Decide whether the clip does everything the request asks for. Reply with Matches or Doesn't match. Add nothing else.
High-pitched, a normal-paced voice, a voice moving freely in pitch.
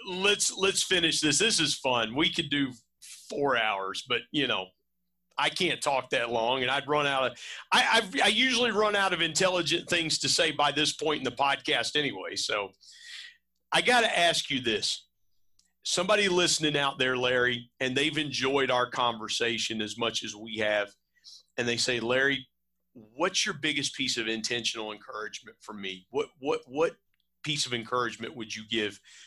Doesn't match